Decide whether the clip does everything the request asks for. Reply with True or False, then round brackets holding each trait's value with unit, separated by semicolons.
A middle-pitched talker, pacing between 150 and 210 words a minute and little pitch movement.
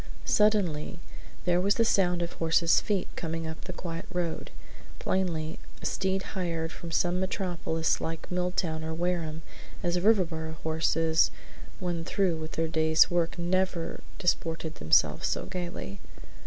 False (170 Hz; 140 wpm; 2.2 semitones)